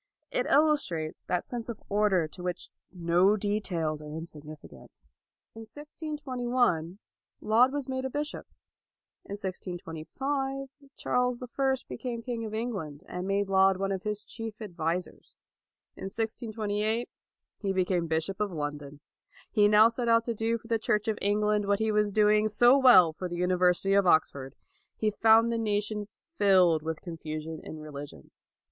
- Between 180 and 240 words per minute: No, average, 155 wpm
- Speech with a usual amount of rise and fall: Yes, average, 4.7 semitones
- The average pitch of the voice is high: Yes, high, 205 Hz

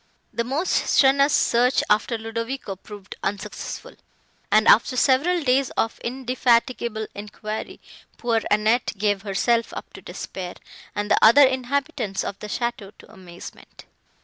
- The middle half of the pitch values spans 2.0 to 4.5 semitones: Yes, average, 3.8 semitones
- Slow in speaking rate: Yes, slow, 130 wpm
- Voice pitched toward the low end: No, high, 230 Hz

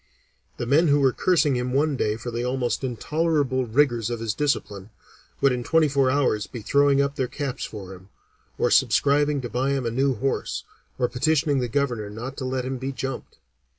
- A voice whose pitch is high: No, low, 130 Hz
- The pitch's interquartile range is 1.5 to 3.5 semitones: Yes, average, 2.8 semitones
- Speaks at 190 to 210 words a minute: Yes, average, 200 wpm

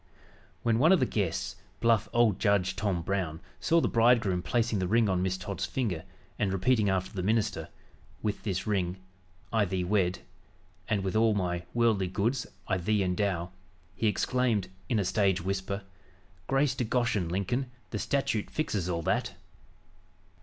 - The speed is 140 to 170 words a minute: Yes, average, 160 wpm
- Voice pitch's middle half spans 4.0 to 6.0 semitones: No, average, 3.6 semitones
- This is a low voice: Yes, low, 100 Hz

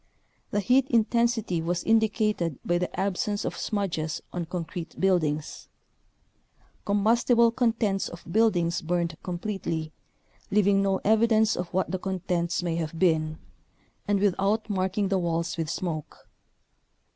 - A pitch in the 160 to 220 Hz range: Yes, high, 190 Hz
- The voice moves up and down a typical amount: Yes, average, 3.9 semitones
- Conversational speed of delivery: No, slow, 130 wpm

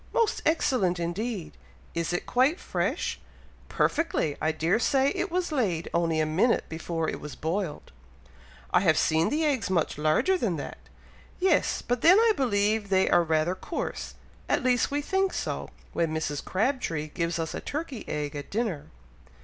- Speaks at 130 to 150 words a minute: No, average, 165 wpm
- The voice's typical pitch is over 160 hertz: Yes, high, 190 Hz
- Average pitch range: No, wide, 9.0 semitones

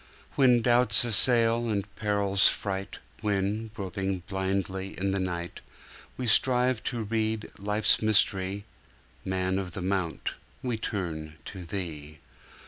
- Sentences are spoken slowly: Yes, slow, 115 wpm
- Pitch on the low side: Yes, low, 100 Hz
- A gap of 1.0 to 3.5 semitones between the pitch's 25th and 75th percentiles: Yes, average, 2.8 semitones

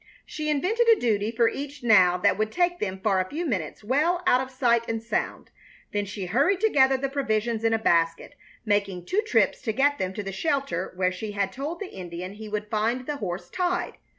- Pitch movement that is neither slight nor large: No, wide, 6.2 semitones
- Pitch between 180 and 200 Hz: No, high, 225 Hz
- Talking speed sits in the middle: No, fast, 215 wpm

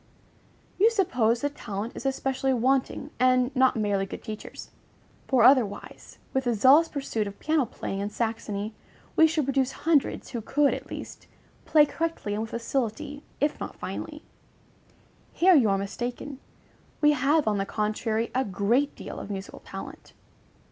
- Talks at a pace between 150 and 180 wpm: Yes, average, 155 wpm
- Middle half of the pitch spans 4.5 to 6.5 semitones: Yes, average, 5.0 semitones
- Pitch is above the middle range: Yes, very high, 255 Hz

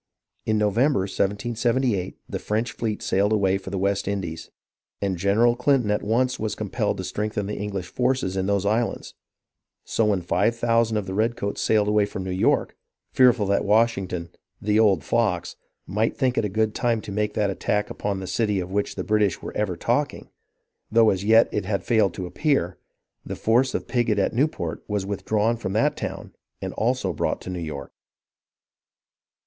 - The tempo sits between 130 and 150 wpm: No, average, 185 wpm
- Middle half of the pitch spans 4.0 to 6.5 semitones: No, average, 2.9 semitones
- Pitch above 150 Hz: No, low, 105 Hz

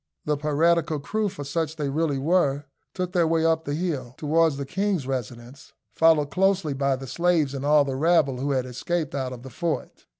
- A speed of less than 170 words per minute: No, average, 200 wpm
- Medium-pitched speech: Yes, medium, 150 Hz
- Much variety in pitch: No, average, 3.5 semitones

